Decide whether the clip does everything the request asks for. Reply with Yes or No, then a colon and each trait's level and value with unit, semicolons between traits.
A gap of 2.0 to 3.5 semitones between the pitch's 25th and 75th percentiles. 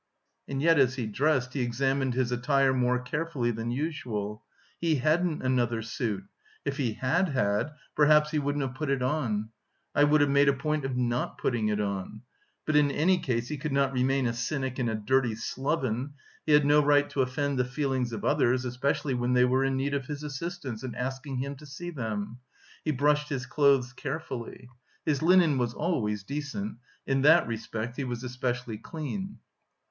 Yes: average, 3.2 semitones